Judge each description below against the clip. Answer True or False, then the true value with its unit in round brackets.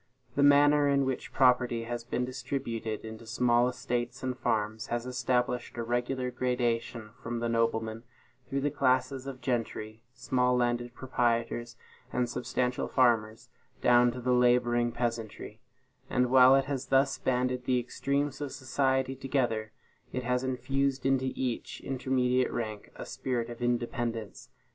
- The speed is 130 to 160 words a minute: True (140 wpm)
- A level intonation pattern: True (1.7 semitones)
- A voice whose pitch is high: False (125 Hz)